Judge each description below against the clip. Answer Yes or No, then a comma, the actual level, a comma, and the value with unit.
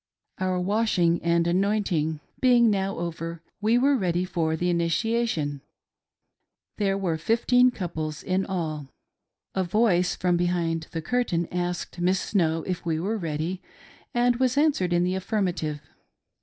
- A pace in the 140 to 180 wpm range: Yes, average, 145 wpm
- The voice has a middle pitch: Yes, medium, 180 Hz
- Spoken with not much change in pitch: No, average, 3.9 semitones